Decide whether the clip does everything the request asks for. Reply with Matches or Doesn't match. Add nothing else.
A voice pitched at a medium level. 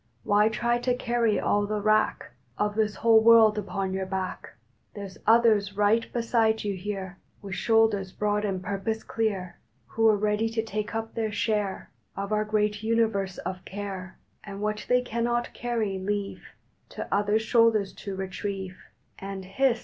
Doesn't match